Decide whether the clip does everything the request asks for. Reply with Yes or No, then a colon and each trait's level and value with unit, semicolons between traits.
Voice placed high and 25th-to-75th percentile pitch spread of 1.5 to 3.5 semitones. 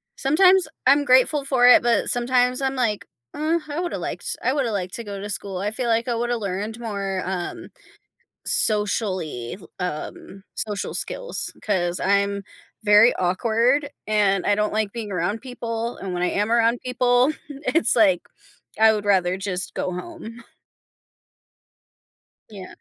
No: high, 220 Hz; average, 4.1 semitones